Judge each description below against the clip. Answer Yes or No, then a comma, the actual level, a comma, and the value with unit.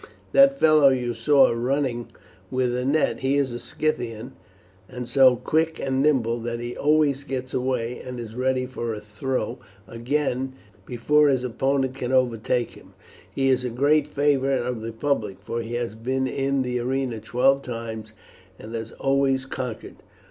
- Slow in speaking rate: No, average, 165 wpm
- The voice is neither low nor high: No, low, 130 Hz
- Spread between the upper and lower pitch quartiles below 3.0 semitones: Yes, narrow, 2.5 semitones